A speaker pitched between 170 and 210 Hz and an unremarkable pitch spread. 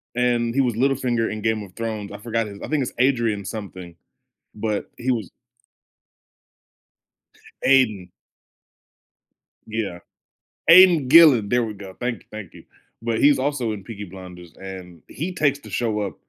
No: low, 115 Hz; average, 4.0 semitones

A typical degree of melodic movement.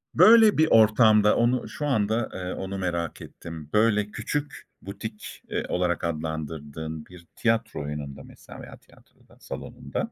No: wide, 5.9 semitones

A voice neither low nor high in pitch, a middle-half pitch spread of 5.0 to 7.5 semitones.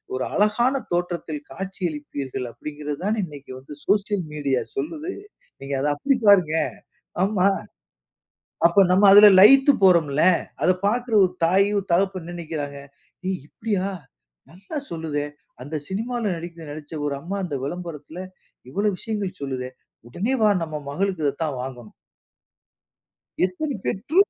Yes: medium, 175 Hz; wide, 5.5 semitones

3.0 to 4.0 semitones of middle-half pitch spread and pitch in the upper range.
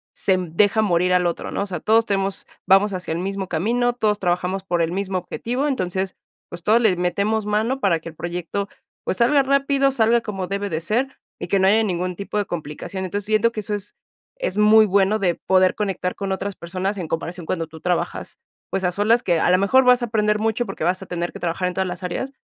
Yes: average, 3.3 semitones; high, 195 Hz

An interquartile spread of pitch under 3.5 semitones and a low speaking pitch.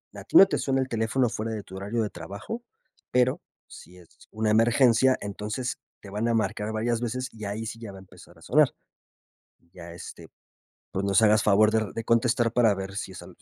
Yes: average, 2.9 semitones; low, 110 Hz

